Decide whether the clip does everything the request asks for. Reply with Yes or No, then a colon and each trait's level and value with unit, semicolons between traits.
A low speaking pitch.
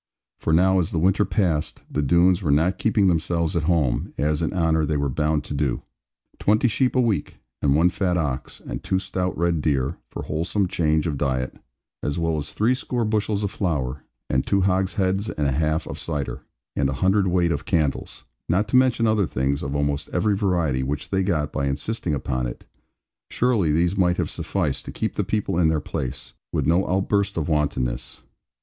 Yes: very low, 85 Hz